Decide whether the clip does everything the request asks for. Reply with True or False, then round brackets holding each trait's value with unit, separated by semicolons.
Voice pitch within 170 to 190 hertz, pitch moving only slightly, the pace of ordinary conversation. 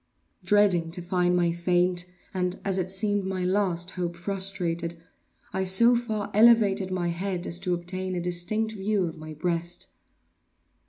True (185 Hz; 2.2 semitones; 155 wpm)